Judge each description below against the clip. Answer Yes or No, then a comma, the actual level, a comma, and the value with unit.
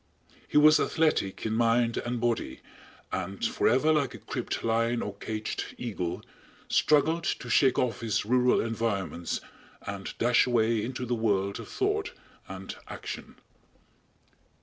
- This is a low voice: Yes, low, 115 Hz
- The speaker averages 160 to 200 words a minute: No, slow, 135 wpm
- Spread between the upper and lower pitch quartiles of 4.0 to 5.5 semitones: No, average, 2.9 semitones